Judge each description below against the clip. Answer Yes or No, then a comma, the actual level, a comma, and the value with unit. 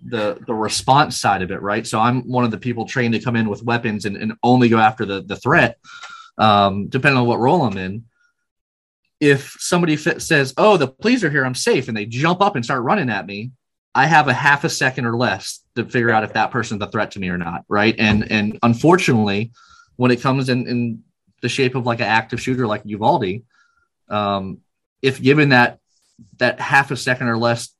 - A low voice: Yes, low, 120 Hz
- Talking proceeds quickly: Yes, fast, 220 wpm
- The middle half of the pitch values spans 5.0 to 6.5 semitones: No, average, 4.1 semitones